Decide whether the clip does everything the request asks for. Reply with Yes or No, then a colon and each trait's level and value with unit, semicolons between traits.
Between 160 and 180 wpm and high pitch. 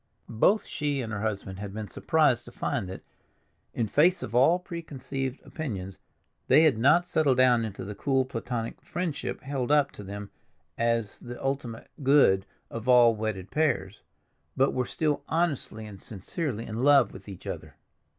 No: average, 165 wpm; low, 125 Hz